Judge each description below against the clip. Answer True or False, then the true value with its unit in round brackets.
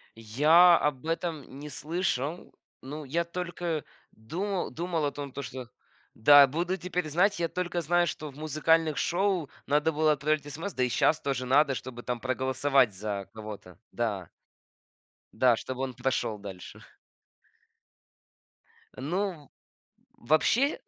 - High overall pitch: False (150 Hz)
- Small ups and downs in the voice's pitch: False (4.8 semitones)